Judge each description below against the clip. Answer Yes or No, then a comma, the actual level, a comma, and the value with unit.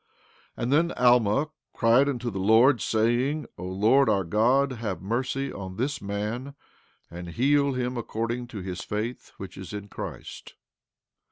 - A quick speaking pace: No, average, 155 wpm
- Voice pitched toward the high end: No, low, 115 Hz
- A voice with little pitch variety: No, average, 4.4 semitones